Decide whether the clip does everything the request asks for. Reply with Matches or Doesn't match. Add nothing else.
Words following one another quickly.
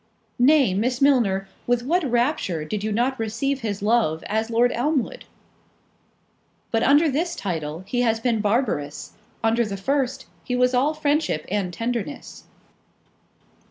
Doesn't match